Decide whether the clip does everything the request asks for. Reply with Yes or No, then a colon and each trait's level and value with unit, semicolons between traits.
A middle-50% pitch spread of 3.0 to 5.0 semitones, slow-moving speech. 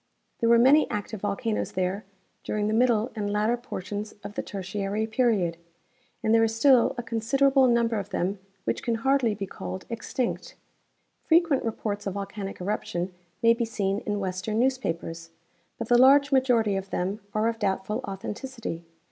No: average, 3.3 semitones; average, 165 wpm